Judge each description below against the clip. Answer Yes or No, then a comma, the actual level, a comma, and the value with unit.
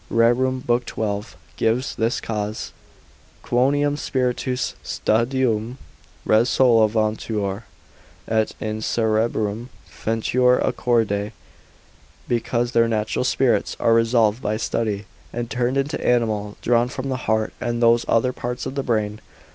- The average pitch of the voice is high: No, low, 115 Hz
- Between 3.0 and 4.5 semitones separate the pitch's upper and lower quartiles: No, narrow, 2.4 semitones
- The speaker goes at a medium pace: No, slow, 120 wpm